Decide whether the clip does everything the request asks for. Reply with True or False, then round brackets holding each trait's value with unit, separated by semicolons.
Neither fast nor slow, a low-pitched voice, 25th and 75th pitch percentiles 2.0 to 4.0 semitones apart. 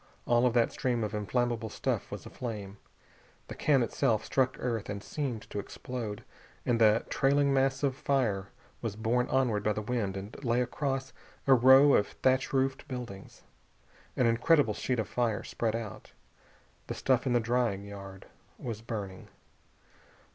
True (155 wpm; 120 Hz; 3.5 semitones)